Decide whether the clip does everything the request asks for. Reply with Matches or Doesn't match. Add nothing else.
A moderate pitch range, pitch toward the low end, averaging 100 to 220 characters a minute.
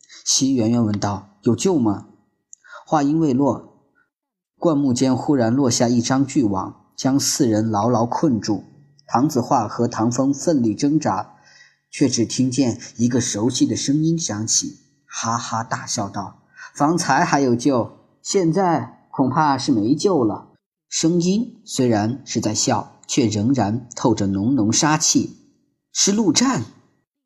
Matches